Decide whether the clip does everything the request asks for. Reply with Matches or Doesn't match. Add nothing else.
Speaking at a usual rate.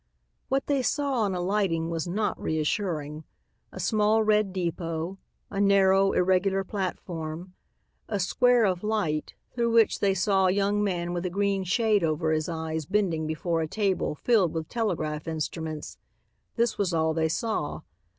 Matches